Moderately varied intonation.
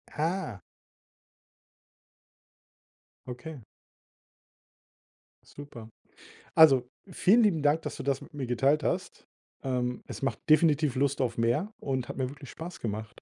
Yes: average, 4.0 semitones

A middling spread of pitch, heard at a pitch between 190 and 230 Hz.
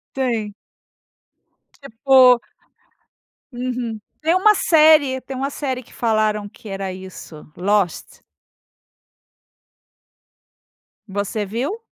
No: average, 4.6 semitones; high, 240 Hz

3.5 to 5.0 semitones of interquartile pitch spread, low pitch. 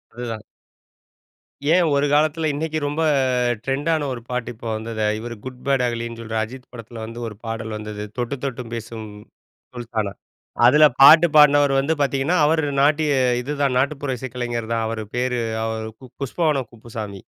Yes: average, 4.1 semitones; low, 125 Hz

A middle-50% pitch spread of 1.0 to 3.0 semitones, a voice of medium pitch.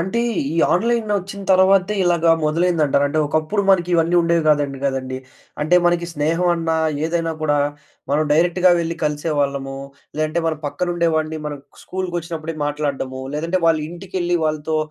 Yes: average, 2.7 semitones; medium, 165 Hz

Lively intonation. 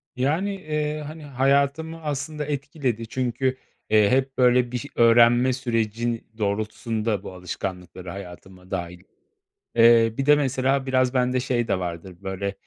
No: average, 4.4 semitones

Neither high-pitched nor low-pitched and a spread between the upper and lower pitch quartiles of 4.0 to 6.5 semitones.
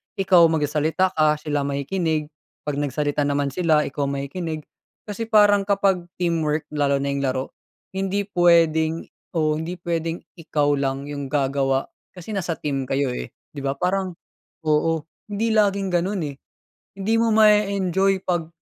Yes: medium, 160 Hz; average, 4.7 semitones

